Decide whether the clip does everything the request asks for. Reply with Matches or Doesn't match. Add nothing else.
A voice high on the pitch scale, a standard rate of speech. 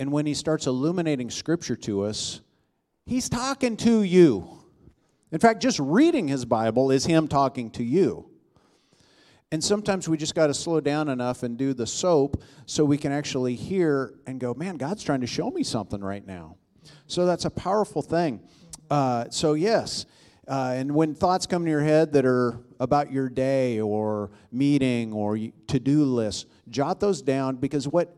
Doesn't match